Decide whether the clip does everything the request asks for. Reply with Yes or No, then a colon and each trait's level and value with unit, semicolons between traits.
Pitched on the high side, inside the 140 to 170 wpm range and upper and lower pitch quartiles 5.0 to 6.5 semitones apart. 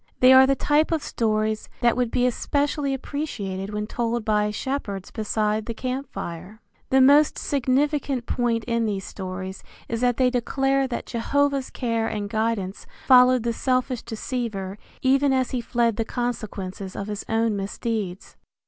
No: high, 235 Hz; average, 155 wpm; average, 3.7 semitones